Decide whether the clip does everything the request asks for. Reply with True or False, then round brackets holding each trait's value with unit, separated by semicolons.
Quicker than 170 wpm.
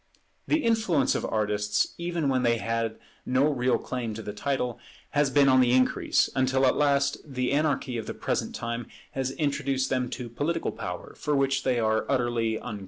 True (185 wpm)